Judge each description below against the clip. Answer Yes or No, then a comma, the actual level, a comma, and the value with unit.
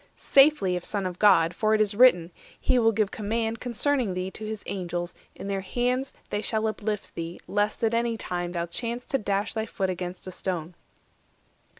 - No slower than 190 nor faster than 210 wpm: Yes, average, 195 wpm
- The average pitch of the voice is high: Yes, high, 205 Hz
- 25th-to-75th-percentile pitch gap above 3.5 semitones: Yes, average, 3.9 semitones